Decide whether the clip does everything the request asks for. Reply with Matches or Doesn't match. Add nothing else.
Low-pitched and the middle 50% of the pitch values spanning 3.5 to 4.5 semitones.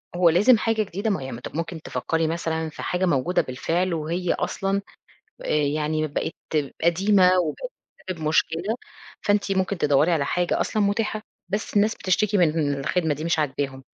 Doesn't match